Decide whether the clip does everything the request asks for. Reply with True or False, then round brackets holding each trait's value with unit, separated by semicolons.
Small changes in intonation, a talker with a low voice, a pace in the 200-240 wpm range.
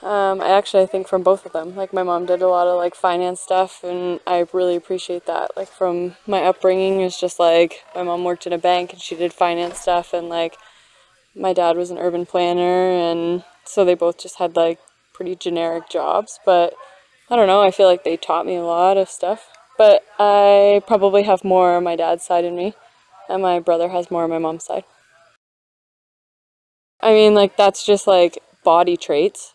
False (1.7 semitones; 180 Hz; 205 wpm)